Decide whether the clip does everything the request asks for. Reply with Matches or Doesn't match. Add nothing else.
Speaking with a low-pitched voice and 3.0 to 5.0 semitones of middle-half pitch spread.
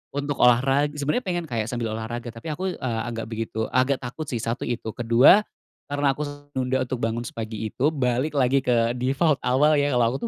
Matches